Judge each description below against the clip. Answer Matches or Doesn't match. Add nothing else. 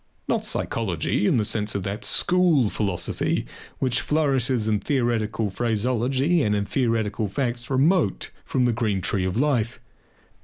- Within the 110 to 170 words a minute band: Matches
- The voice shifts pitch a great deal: Doesn't match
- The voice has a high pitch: Doesn't match